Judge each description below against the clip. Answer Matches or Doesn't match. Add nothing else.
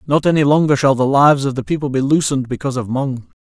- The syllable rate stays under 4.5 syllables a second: Doesn't match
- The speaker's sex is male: Matches